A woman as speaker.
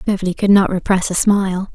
Yes: female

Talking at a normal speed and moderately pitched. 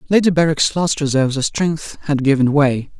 Yes: average, 180 wpm; medium, 150 Hz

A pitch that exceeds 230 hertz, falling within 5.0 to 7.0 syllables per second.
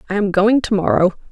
No: high, 195 Hz; 5.8 syllables/s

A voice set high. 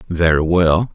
No: very low, 85 Hz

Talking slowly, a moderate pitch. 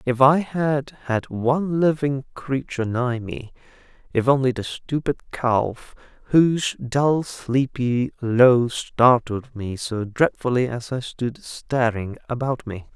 No: slow, 125 wpm; low, 125 Hz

